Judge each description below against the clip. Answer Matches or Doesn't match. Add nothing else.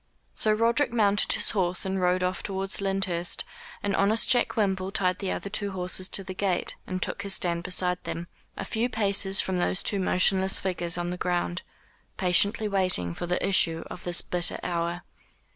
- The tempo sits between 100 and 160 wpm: Doesn't match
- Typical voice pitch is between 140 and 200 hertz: Matches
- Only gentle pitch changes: Matches